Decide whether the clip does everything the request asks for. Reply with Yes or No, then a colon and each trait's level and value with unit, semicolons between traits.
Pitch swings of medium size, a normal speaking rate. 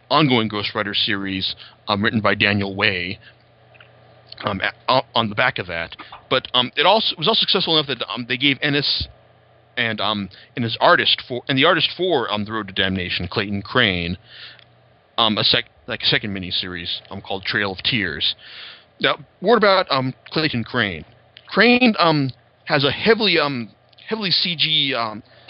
No: wide, 5.9 semitones; average, 175 wpm